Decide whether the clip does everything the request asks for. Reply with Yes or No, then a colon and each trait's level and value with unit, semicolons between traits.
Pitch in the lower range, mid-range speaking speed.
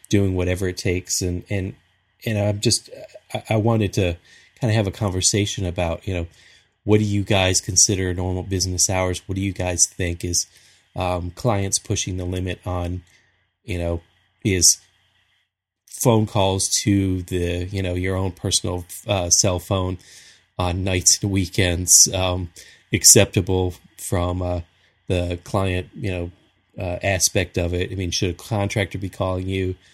Yes: very low, 95 Hz; average, 160 wpm